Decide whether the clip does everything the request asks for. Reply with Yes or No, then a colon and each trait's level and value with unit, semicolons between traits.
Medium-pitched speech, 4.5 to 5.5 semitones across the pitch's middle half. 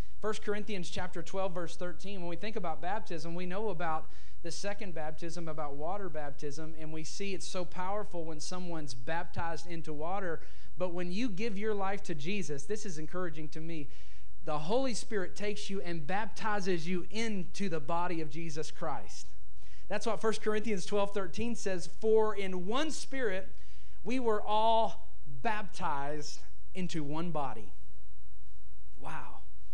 Yes: medium, 175 Hz; average, 4.8 semitones